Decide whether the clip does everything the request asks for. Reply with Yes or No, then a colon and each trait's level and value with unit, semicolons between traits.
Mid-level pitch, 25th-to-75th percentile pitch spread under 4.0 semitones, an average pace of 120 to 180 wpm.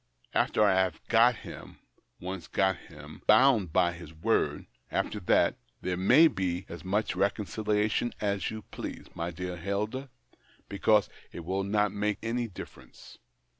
No: low, 100 Hz; average, 3.0 semitones; average, 165 wpm